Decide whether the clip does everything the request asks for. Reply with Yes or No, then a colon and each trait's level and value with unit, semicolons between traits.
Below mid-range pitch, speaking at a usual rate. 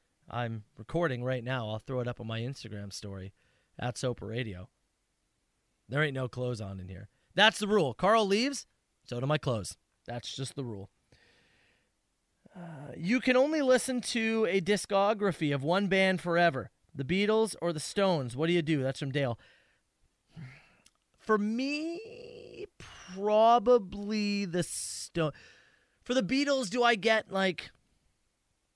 No: medium, 170 Hz; average, 150 wpm